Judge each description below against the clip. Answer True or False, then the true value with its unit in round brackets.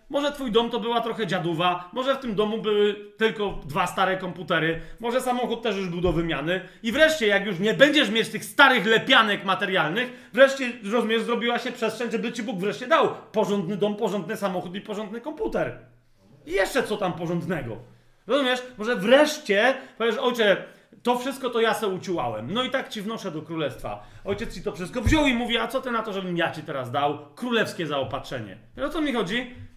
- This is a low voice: False (215 Hz)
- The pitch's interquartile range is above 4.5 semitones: True (4.9 semitones)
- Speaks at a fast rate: True (195 wpm)